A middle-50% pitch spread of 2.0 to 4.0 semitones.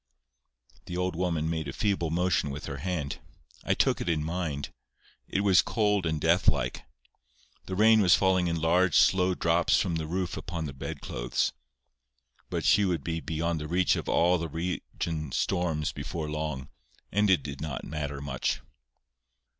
Yes: average, 3.0 semitones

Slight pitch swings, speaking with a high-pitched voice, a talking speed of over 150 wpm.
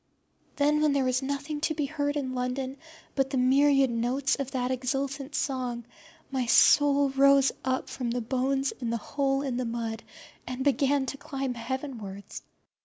Yes: narrow, 1.9 semitones; very high, 270 Hz; average, 170 wpm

